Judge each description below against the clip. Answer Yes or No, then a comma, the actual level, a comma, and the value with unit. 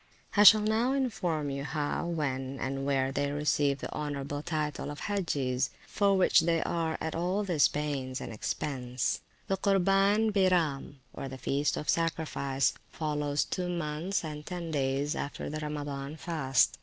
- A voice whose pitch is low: No, medium, 150 Hz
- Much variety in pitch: No, average, 4.2 semitones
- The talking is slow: No, average, 155 wpm